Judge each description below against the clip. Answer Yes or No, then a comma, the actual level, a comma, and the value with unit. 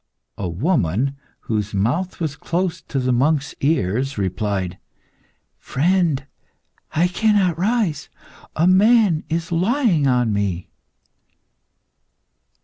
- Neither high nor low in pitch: Yes, medium, 150 Hz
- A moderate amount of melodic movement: No, wide, 8.5 semitones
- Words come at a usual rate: No, slow, 100 wpm